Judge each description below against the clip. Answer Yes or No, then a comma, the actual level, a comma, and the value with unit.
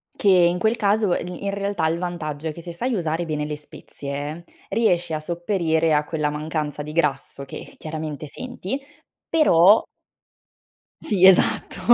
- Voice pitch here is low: No, medium, 170 Hz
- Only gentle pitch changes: No, average, 3.9 semitones